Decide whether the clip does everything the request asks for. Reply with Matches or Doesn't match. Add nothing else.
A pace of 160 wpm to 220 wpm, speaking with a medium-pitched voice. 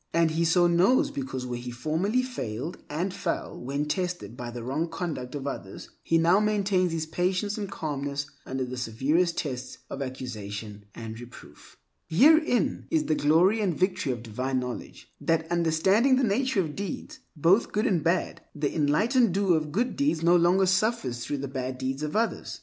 Matches